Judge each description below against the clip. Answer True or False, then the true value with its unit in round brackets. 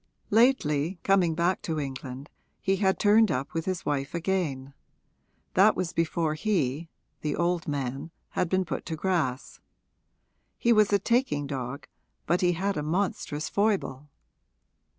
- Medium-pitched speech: True (165 Hz)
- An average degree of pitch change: True (4.9 semitones)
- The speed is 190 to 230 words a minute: False (145 wpm)